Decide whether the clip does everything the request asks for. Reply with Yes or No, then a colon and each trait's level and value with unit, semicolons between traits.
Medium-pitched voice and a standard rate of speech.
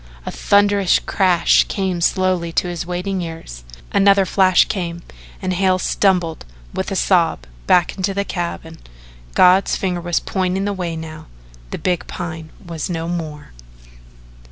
Yes: medium, 180 Hz; average, 145 wpm